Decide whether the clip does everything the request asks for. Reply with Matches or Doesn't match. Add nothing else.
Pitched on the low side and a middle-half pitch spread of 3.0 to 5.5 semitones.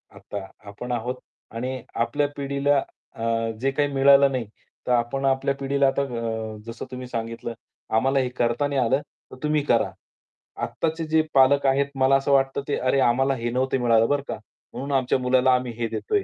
Doesn't match